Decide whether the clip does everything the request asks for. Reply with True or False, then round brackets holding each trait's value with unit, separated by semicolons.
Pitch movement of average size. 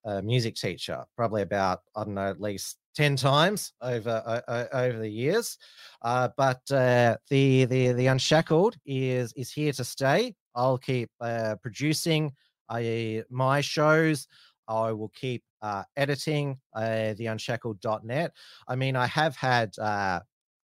True (3.8 semitones)